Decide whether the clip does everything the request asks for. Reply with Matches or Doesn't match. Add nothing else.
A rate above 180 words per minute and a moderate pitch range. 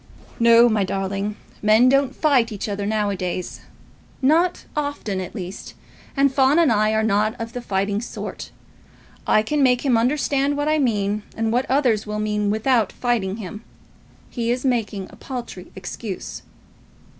Doesn't match